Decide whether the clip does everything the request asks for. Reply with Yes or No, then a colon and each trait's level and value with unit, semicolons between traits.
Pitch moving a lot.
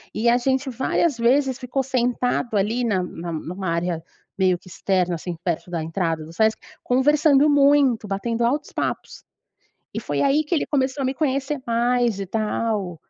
Yes: wide, 6.3 semitones